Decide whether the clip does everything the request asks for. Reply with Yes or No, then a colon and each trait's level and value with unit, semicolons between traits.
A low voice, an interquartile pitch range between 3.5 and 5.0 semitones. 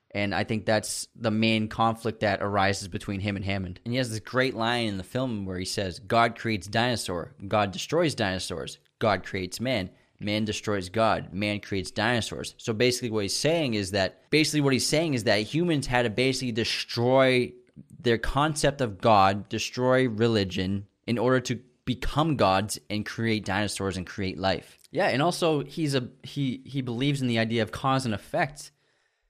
Yes: low, 110 Hz; average, 3.9 semitones